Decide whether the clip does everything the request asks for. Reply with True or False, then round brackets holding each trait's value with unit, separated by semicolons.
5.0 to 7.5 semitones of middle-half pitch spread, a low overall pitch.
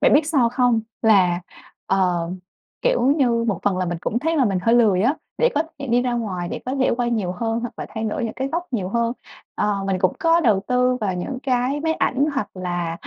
False (5.4 semitones; 235 Hz)